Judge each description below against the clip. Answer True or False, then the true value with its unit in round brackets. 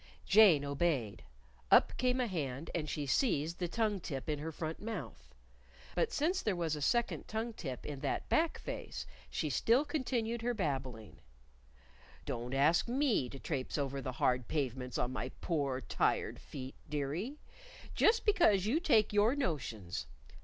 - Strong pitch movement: True (9.0 semitones)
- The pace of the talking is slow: False (160 wpm)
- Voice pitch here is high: False (160 Hz)